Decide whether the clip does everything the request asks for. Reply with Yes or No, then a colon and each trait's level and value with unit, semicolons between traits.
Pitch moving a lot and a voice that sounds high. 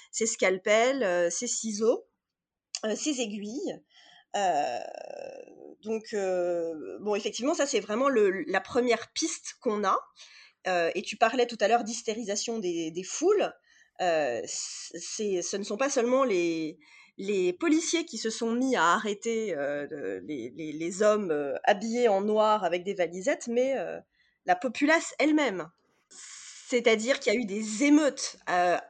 Yes: wide, 6.1 semitones; high, 225 Hz